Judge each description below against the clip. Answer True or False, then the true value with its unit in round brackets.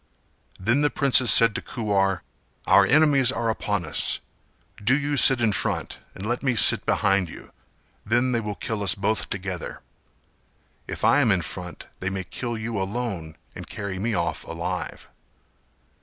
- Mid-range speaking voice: False (110 Hz)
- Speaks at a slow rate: False (165 wpm)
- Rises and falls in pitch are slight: False (4.1 semitones)